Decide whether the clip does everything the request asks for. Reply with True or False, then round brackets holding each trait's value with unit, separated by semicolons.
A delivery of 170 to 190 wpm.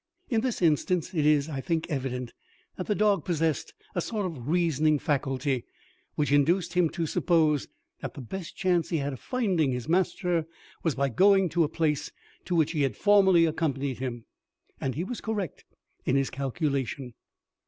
True (175 wpm)